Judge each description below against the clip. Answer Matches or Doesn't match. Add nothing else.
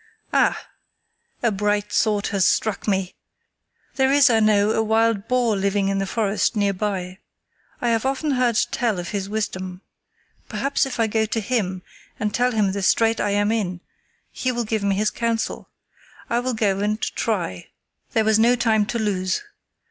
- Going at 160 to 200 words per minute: Matches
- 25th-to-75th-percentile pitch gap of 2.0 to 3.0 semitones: Matches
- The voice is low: Doesn't match